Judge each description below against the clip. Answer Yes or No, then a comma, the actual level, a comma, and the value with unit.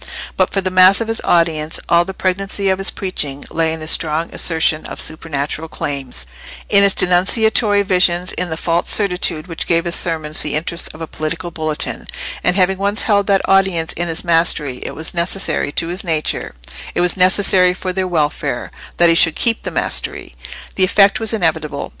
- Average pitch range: Yes, average, 3.2 semitones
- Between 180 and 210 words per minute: Yes, average, 185 wpm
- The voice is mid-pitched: Yes, medium, 175 Hz